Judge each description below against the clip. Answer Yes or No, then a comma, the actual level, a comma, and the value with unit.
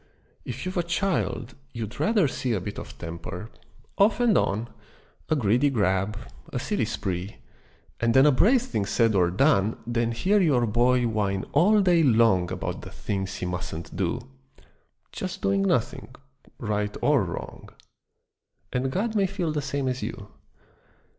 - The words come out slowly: No, average, 160 wpm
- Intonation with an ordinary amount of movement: No, wide, 7.8 semitones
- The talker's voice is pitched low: Yes, low, 120 Hz